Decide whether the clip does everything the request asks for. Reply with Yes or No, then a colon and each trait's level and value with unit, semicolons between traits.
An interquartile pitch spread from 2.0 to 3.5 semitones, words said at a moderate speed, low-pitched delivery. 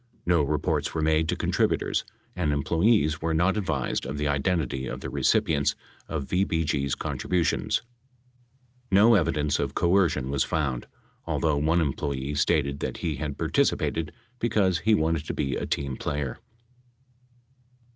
Yes: average, 3.2 semitones; average, 145 wpm; very low, 75 Hz